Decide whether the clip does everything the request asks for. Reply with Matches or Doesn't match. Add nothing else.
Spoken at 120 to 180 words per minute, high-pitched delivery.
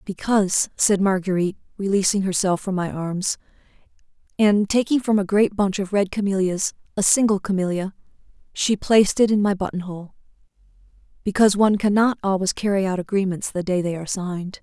Matches